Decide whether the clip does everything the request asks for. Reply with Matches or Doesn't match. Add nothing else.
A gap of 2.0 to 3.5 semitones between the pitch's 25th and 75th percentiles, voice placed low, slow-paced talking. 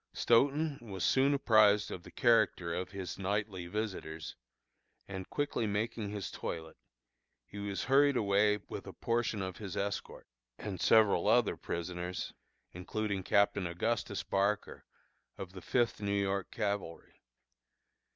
Matches